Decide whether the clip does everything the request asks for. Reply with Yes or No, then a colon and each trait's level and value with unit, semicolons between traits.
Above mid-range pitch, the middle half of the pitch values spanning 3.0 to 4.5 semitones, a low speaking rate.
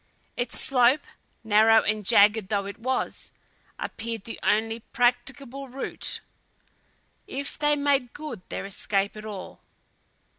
Yes: high, 230 Hz; average, 3.9 semitones; slow, 120 wpm